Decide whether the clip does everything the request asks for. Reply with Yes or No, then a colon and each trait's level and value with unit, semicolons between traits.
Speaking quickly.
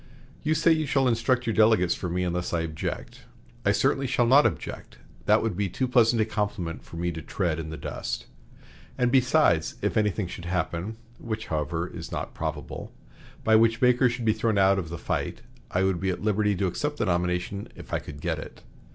Yes: fast, 210 wpm